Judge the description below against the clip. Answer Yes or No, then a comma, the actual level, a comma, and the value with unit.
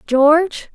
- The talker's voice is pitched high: Yes, very high, 305 Hz